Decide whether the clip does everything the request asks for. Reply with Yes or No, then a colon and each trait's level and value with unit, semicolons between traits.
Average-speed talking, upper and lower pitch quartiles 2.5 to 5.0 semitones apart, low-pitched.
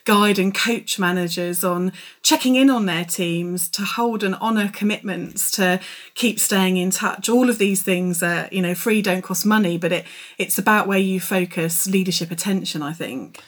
No: average, 185 wpm; average, 2.8 semitones; high, 190 Hz